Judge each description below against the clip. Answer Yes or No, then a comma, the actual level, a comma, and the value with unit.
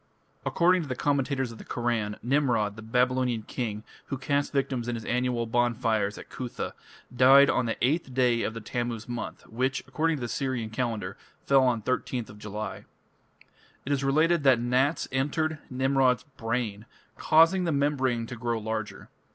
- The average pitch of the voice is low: Yes, low, 125 Hz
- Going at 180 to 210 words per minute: No, average, 165 wpm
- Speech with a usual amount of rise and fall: Yes, average, 3.1 semitones